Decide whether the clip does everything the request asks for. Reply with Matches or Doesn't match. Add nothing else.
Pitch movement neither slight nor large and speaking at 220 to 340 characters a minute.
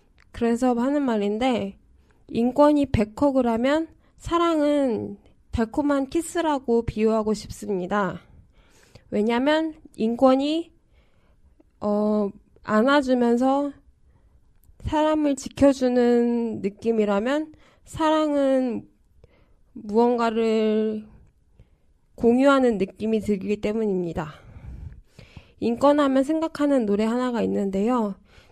Doesn't match